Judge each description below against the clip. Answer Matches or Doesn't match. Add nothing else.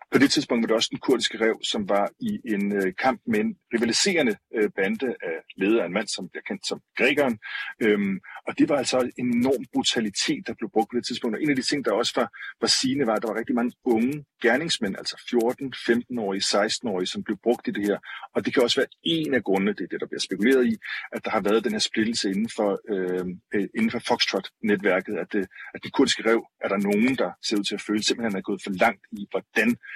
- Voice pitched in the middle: Doesn't match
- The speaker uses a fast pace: Matches